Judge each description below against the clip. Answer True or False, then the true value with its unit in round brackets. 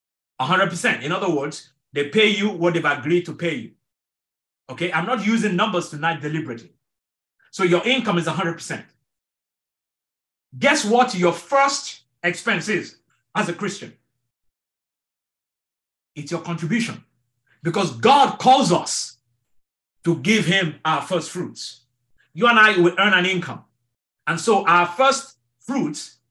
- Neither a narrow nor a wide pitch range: False (6.1 semitones)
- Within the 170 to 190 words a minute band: False (135 wpm)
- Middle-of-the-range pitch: True (175 Hz)